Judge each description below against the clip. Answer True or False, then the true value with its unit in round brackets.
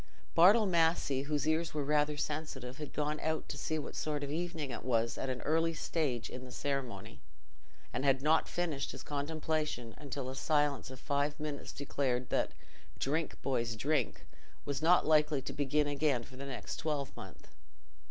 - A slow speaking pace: False (170 wpm)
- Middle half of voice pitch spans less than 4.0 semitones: True (2.8 semitones)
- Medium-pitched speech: True (145 Hz)